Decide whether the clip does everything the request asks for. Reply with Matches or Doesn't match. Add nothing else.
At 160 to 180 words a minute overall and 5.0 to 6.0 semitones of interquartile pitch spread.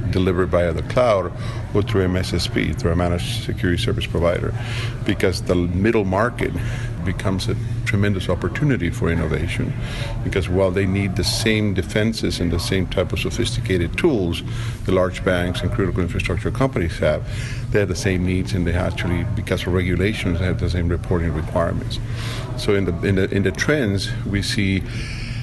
Doesn't match